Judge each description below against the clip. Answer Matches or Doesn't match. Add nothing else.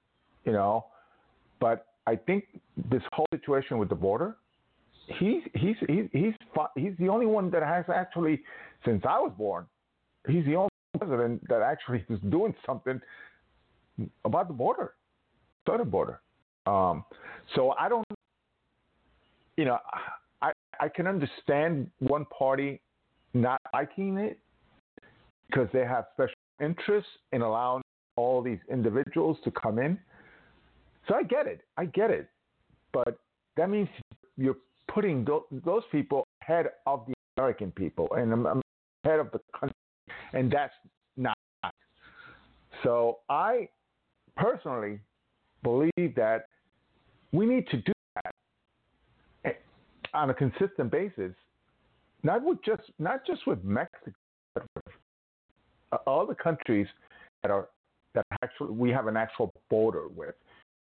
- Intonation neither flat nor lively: Doesn't match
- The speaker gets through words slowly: Matches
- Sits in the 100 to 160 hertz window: Matches